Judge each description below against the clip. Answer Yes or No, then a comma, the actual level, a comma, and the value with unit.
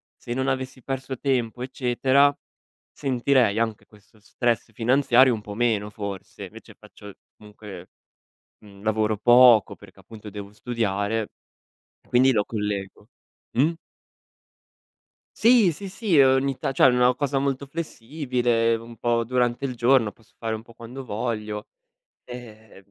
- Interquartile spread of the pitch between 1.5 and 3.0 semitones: No, average, 3.5 semitones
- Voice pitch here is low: Yes, low, 120 Hz